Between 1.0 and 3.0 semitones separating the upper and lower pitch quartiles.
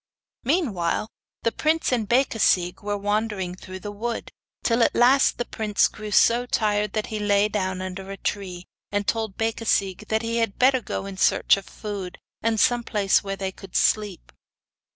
Yes: average, 2.7 semitones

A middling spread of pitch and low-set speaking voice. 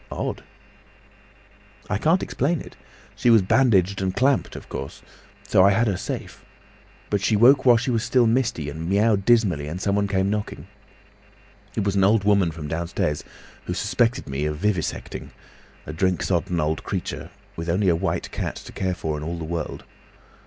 Yes: average, 4.9 semitones; low, 100 Hz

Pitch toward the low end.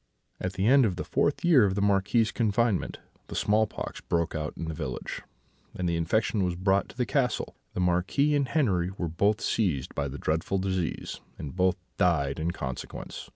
Yes: very low, 95 Hz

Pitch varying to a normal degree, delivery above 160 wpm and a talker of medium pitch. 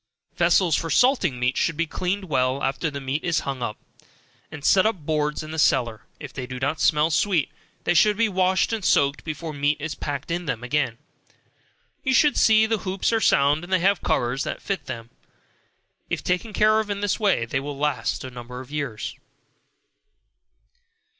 No: wide, 5.7 semitones; average, 195 wpm; medium, 155 Hz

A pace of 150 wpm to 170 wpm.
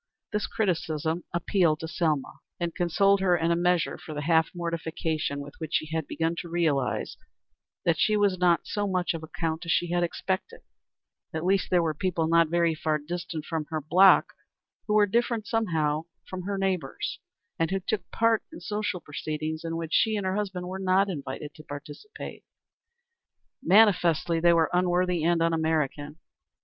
No: average, 180 wpm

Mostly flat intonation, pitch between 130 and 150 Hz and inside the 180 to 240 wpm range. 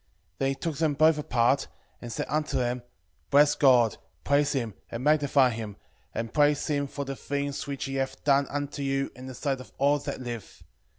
Yes: narrow, 2.2 semitones; medium, 140 Hz; average, 200 wpm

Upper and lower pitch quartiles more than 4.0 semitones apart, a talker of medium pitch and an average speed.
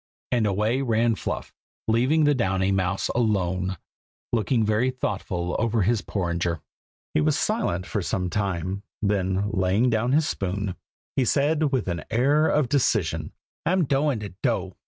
No: average, 5.2 semitones; low, 105 Hz; average, 150 wpm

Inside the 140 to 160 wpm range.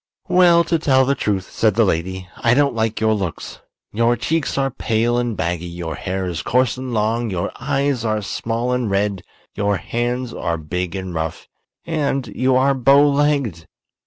No: average, 180 wpm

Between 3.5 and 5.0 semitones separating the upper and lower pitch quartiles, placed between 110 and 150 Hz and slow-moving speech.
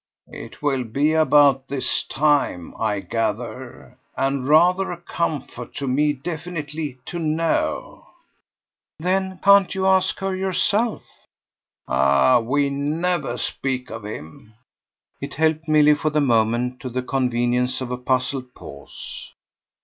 Yes: average, 4.3 semitones; medium, 140 Hz; slow, 125 wpm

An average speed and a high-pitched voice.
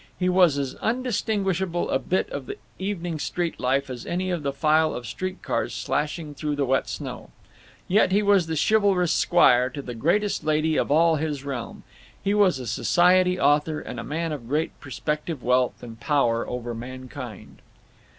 No: average, 180 wpm; medium, 155 Hz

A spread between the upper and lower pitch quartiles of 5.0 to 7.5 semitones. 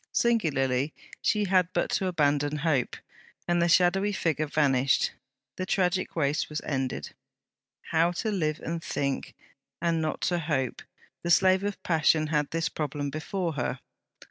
No: average, 3.6 semitones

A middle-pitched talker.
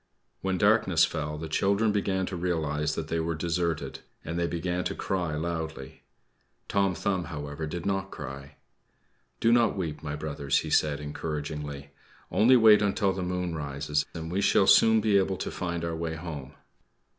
No: very low, 85 Hz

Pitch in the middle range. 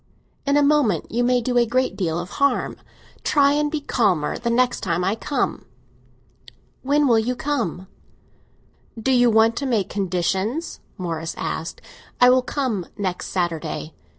No: high, 235 Hz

